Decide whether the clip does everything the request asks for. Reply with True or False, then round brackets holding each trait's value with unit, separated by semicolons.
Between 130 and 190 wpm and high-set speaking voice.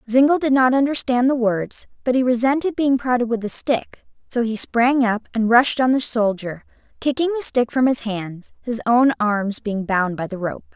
False (205 wpm; 240 Hz)